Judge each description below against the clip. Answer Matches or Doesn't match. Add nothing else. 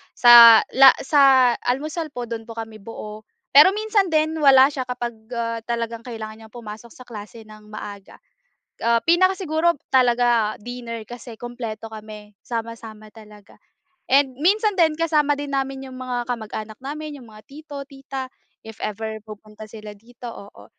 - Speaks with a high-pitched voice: Matches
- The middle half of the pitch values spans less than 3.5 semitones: Doesn't match